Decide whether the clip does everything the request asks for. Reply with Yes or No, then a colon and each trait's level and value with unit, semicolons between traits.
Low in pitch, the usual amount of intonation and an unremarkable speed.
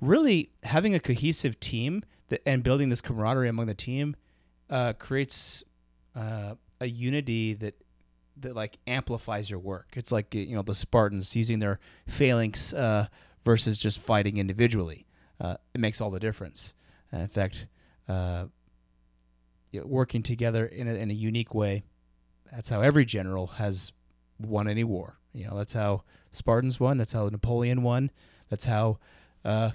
Yes: low, 110 Hz; average, 3.7 semitones; average, 150 wpm